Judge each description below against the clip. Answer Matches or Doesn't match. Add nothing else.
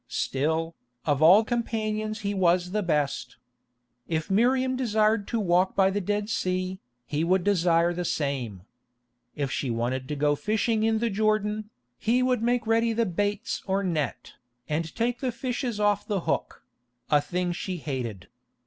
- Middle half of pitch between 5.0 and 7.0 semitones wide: Matches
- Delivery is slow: Doesn't match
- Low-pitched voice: Doesn't match